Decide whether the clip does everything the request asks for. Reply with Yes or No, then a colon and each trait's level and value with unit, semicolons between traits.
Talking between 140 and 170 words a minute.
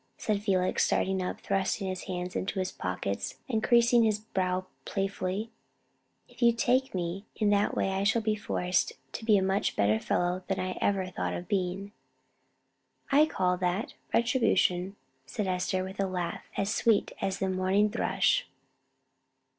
Yes: average, 160 wpm